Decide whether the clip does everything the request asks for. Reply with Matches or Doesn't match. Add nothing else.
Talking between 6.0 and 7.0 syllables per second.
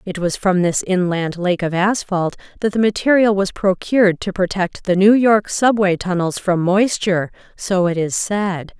Doesn't match